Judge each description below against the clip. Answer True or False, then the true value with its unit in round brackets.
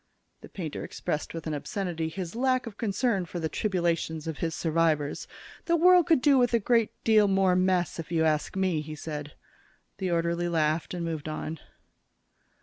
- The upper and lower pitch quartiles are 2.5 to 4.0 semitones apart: False (4.4 semitones)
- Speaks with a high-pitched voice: False (175 Hz)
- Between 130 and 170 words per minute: False (180 wpm)